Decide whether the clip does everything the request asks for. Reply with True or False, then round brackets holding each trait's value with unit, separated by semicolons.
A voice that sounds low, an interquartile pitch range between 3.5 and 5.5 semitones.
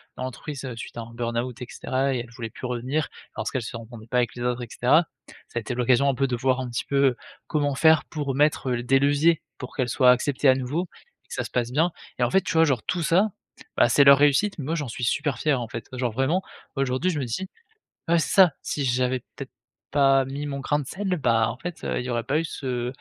False (130 Hz; 3.1 semitones)